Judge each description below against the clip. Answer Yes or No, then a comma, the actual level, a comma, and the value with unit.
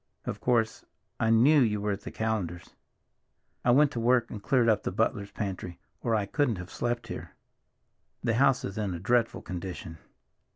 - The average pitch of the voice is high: No, low, 110 Hz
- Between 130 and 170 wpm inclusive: No, average, 180 wpm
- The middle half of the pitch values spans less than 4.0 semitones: Yes, average, 3.4 semitones